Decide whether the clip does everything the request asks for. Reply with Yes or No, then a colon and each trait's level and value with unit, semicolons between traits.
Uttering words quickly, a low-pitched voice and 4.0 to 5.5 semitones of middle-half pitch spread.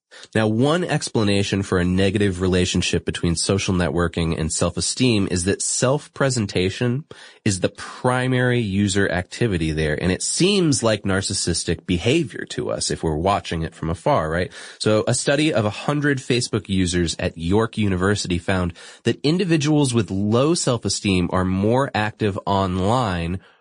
No: average, 145 wpm; low, 100 Hz; average, 5.2 semitones